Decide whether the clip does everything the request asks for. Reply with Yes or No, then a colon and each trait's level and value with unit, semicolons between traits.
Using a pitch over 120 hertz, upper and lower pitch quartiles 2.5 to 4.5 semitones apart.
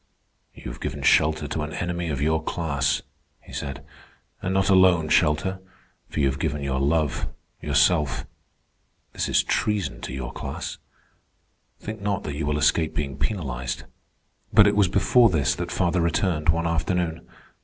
No: very low, 80 Hz; average, 4.0 semitones